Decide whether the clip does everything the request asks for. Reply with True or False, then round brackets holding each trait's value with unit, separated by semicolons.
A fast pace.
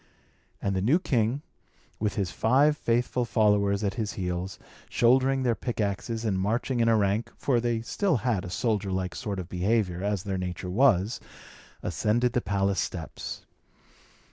False (160 wpm)